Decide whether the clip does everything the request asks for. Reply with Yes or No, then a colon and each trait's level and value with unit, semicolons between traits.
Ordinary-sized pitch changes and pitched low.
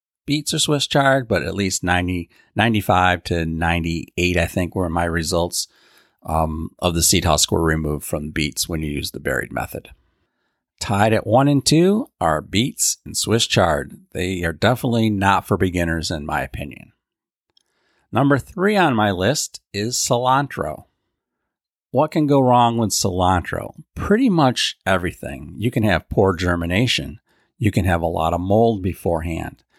No: wide, 6.3 semitones; very low, 95 Hz